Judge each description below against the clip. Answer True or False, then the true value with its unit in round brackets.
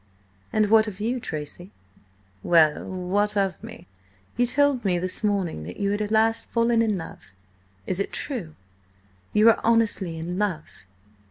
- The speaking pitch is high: True (205 Hz)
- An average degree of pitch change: True (4.1 semitones)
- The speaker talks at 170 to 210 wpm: False (160 wpm)